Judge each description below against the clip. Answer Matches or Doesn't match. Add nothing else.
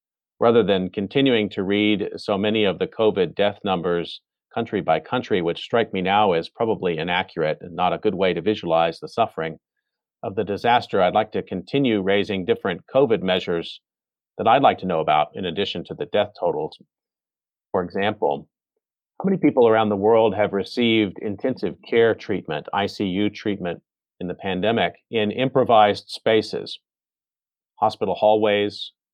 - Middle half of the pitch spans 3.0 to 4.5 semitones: Doesn't match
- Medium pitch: Doesn't match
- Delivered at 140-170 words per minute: Matches